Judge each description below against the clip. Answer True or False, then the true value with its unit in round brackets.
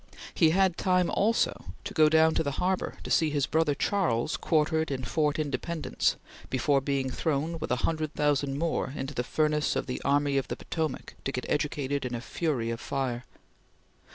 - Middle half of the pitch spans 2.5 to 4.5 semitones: True (2.9 semitones)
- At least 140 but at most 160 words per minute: False (180 wpm)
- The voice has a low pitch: False (150 Hz)